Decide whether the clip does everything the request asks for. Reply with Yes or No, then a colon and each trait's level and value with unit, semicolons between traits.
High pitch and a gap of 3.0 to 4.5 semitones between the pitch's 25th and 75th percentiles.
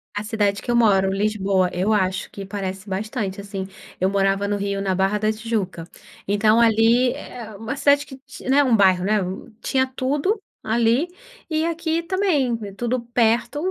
Yes: high, 215 Hz; average, 4.2 semitones